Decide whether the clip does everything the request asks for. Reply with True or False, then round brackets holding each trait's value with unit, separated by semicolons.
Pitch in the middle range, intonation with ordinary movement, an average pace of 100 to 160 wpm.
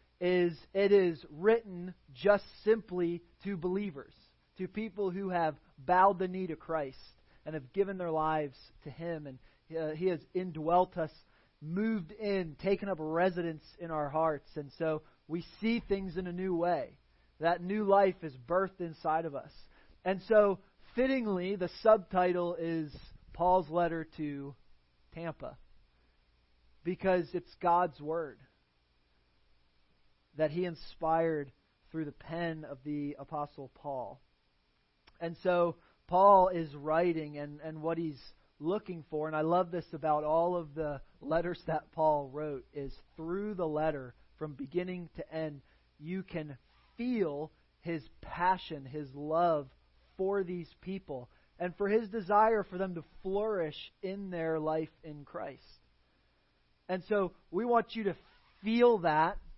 True (165 Hz; 3.7 semitones; 140 wpm)